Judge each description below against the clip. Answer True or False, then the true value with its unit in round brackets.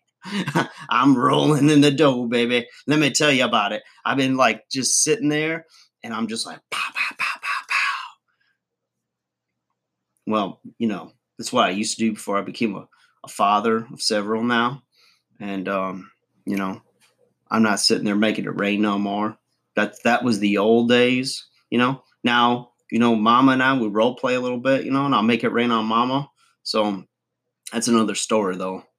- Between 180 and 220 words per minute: True (190 wpm)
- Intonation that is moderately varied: True (4.1 semitones)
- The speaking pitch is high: False (120 Hz)